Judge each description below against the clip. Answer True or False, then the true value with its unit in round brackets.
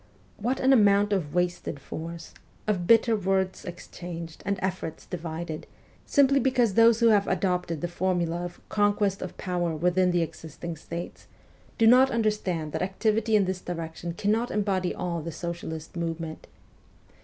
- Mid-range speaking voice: True (180 Hz)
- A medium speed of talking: True (165 wpm)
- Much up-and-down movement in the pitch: False (3.6 semitones)